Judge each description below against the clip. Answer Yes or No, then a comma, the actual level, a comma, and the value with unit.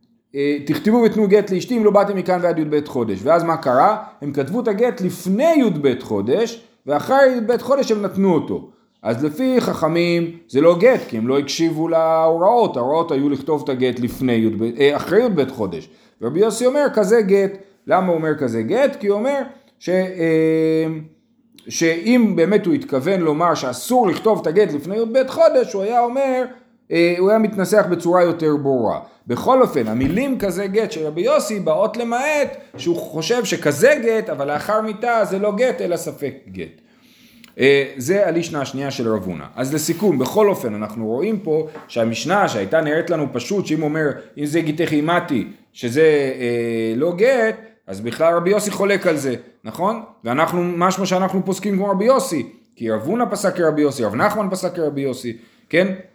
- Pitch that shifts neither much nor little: No, wide, 6.7 semitones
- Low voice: No, medium, 175 Hz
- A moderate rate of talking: No, fast, 175 wpm